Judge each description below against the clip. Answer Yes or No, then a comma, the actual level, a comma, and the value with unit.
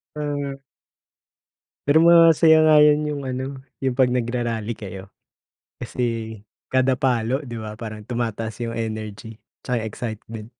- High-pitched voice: No, low, 120 Hz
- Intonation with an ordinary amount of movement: Yes, average, 4.0 semitones